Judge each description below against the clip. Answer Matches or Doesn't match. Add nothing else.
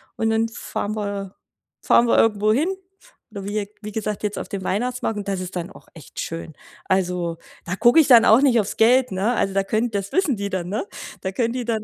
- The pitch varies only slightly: Doesn't match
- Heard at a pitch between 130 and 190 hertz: Doesn't match